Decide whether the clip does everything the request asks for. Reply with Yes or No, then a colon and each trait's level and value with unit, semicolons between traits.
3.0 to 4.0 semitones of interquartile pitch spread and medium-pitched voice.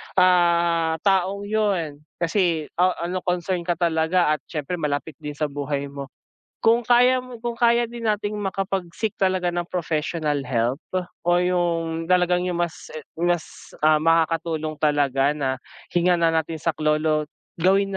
Yes: average, 3.3 semitones; medium, 170 Hz